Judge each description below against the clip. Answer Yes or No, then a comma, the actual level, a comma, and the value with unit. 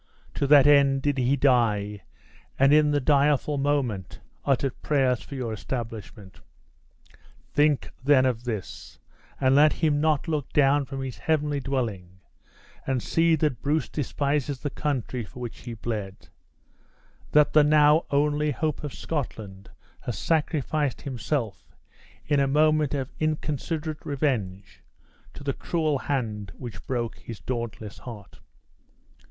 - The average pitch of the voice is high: No, medium, 140 Hz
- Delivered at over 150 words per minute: No, slow, 135 wpm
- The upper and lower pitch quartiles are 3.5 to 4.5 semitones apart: Yes, average, 3.9 semitones